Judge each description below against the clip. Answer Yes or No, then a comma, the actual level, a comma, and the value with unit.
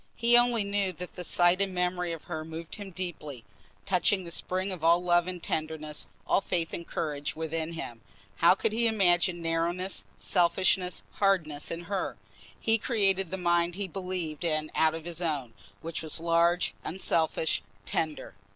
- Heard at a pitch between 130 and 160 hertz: No, medium, 175 Hz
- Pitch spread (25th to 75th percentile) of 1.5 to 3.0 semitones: Yes, narrow, 2.6 semitones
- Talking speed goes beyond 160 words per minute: Yes, average, 170 wpm